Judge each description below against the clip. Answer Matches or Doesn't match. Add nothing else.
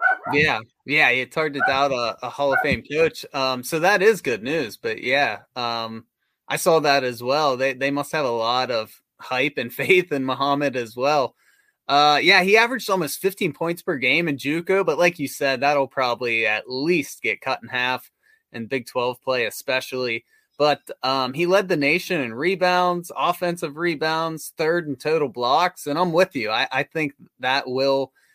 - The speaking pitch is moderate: Matches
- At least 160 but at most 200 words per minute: Matches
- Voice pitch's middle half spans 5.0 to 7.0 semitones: Matches